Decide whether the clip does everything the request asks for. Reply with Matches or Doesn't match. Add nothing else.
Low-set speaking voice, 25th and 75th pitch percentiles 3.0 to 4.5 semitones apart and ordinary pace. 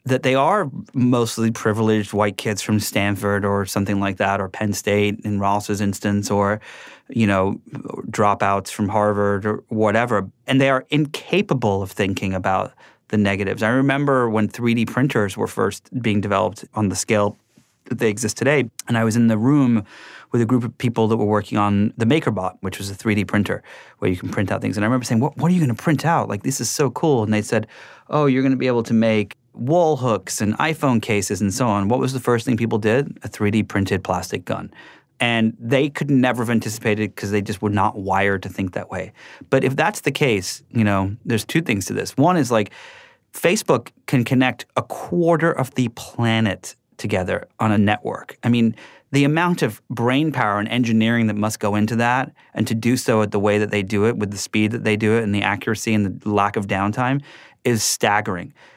Doesn't match